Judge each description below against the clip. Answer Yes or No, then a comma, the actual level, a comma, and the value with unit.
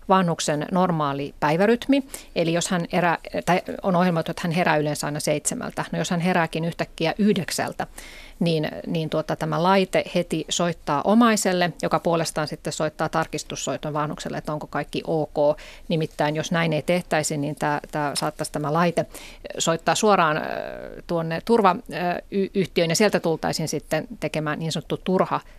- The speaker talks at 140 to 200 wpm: Yes, average, 150 wpm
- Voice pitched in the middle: Yes, medium, 165 Hz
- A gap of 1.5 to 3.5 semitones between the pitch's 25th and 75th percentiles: Yes, average, 2.8 semitones